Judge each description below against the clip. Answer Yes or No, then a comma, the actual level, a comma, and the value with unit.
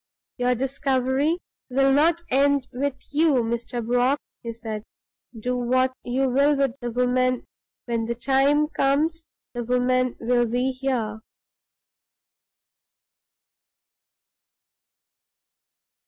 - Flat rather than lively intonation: Yes, narrow, 2.1 semitones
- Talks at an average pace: No, slow, 100 wpm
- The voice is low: No, very high, 255 Hz